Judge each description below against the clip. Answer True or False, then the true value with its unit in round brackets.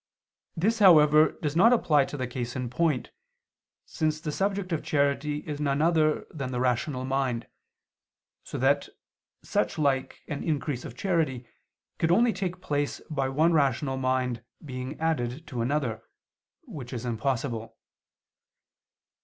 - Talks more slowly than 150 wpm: True (140 wpm)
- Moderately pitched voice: True (145 Hz)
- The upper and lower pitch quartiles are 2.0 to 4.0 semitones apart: True (3.7 semitones)